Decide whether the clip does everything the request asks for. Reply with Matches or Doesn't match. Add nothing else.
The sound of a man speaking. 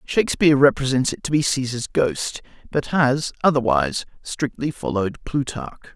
Matches